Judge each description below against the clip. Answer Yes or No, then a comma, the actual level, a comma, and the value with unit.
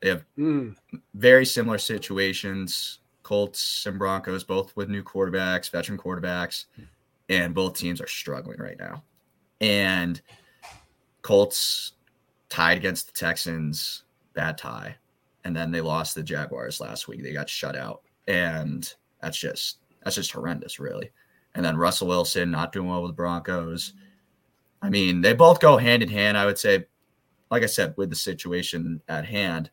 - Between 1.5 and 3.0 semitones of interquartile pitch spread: Yes, average, 2.7 semitones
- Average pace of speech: Yes, average, 155 wpm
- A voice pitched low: Yes, very low, 95 Hz